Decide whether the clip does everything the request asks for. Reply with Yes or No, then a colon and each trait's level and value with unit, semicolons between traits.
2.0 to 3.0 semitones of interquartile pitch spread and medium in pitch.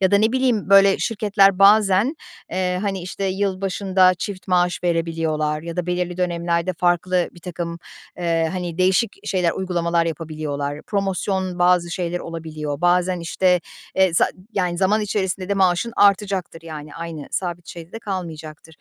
Yes: narrow, 2.4 semitones; medium, 180 Hz